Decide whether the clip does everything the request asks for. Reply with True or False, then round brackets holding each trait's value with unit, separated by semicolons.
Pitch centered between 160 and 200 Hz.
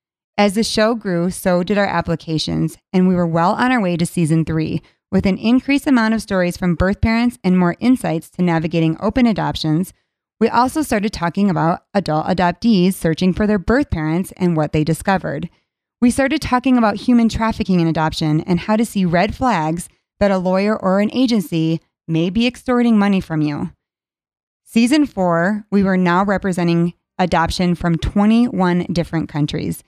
True (185 Hz)